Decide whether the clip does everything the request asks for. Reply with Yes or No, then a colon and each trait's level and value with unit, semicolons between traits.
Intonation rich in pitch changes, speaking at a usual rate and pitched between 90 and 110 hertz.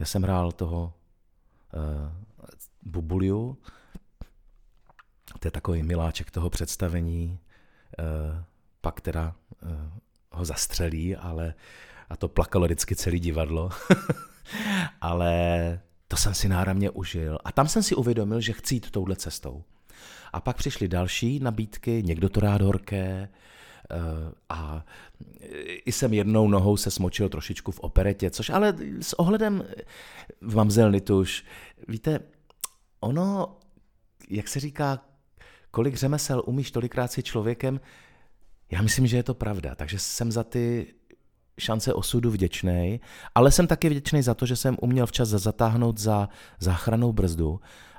Yes: wide, 5.8 semitones; average, 130 wpm; low, 100 Hz